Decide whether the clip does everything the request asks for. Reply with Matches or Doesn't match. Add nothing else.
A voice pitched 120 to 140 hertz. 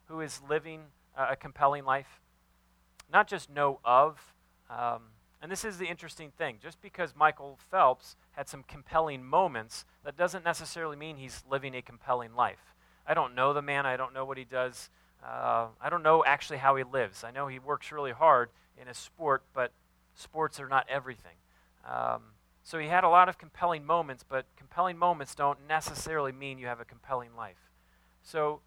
Matches